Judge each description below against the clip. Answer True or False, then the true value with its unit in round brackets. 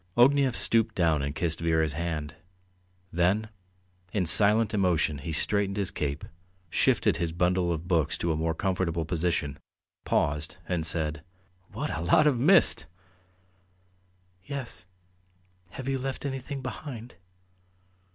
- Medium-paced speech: False (130 wpm)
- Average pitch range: False (5.9 semitones)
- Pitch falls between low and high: False (90 Hz)